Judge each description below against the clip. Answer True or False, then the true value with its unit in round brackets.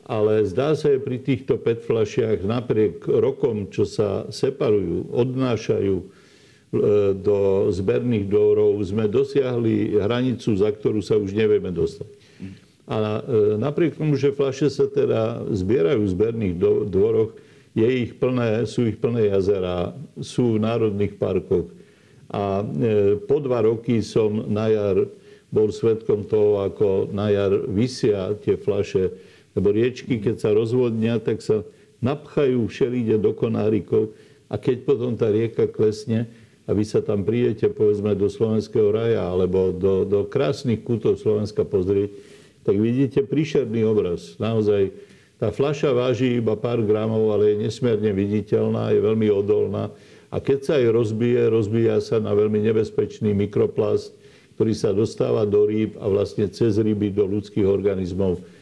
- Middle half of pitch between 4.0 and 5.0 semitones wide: False (2.8 semitones)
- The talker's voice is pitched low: True (110 Hz)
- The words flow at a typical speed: True (140 wpm)